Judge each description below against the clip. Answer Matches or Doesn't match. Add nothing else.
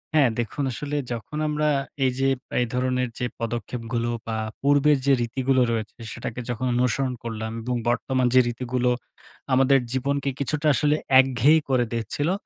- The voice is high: Doesn't match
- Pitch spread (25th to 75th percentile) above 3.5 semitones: Doesn't match